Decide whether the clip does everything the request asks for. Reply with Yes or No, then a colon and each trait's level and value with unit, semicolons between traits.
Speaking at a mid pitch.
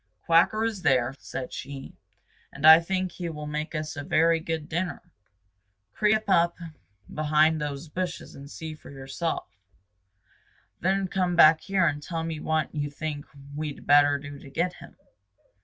Yes: medium, 155 Hz